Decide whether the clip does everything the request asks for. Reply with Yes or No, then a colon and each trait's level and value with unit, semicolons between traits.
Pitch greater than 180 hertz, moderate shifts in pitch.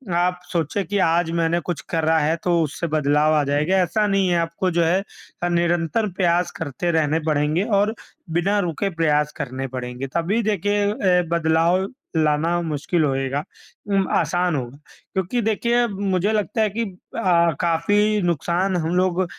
No: medium, 175 Hz; average, 3.4 semitones